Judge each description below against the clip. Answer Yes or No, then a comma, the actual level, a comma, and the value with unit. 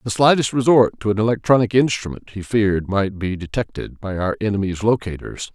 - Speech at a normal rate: Yes, average, 175 wpm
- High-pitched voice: No, low, 105 Hz